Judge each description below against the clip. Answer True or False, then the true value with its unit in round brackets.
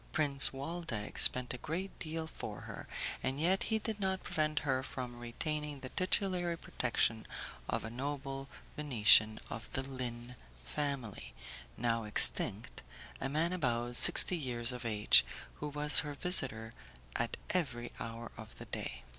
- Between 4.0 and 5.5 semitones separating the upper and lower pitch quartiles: True (4.7 semitones)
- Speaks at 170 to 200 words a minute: False (145 wpm)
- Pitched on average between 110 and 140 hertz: True (135 Hz)